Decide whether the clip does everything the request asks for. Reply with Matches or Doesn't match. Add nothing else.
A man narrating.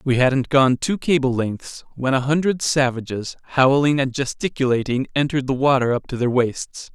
Matches